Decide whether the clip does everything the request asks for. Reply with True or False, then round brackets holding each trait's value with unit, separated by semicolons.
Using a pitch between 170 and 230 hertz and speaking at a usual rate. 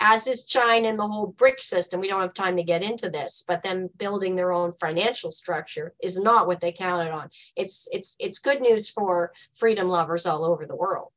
False (190 Hz; 220 wpm)